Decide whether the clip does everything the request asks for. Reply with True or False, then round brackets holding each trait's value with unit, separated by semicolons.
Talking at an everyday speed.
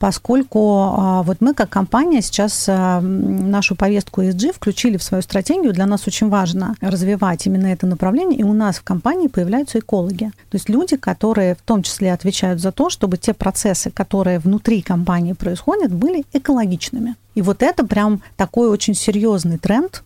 False (165 wpm)